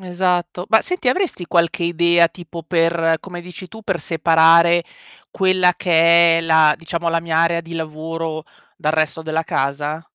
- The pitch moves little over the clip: Yes, narrow, 1.4 semitones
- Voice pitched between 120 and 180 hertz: Yes, medium, 170 Hz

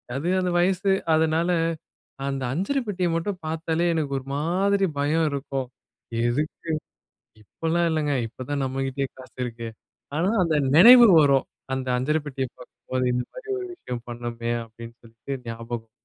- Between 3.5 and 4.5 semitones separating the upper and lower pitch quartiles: No, average, 5.2 semitones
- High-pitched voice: No, medium, 145 Hz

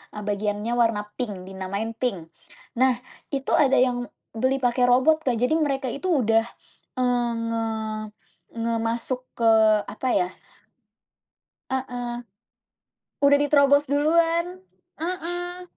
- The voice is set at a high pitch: Yes, very high, 250 Hz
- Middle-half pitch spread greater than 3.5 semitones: Yes, average, 4.0 semitones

